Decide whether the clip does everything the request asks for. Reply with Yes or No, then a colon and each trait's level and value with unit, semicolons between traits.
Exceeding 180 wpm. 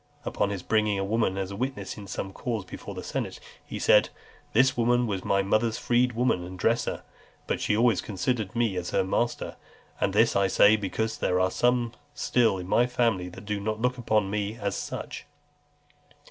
Yes: average, 190 wpm